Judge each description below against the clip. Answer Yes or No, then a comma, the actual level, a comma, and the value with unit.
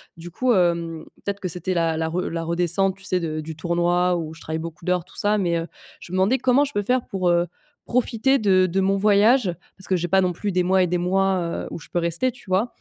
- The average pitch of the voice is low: No, medium, 180 Hz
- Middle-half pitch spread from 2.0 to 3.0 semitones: Yes, average, 2.7 semitones